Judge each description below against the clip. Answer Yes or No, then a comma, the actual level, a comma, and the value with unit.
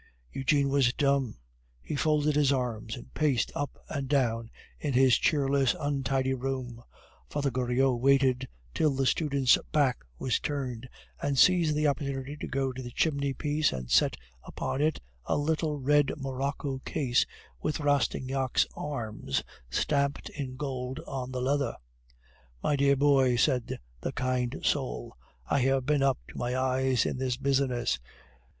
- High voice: No, low, 135 Hz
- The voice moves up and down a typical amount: No, narrow, 2.0 semitones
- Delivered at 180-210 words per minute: No, average, 150 wpm